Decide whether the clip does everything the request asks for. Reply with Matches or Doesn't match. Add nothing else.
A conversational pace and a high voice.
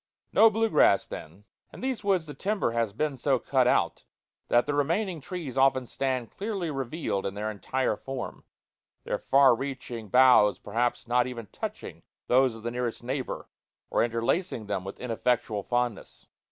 Doesn't match